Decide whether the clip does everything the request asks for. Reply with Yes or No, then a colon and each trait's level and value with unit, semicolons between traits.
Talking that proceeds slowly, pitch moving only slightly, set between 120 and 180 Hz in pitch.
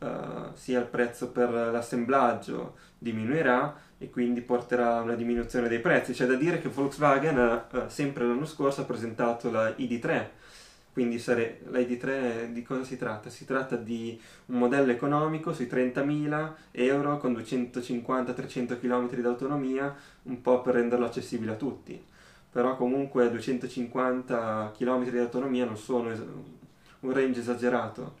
No: average, 150 wpm; narrow, 1.6 semitones; low, 125 Hz